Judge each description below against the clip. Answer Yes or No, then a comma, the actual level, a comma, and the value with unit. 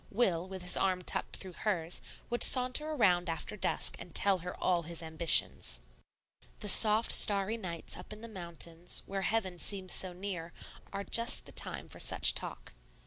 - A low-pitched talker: No, medium, 185 Hz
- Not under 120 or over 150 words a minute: No, average, 175 wpm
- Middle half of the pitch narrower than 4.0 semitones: Yes, average, 3.5 semitones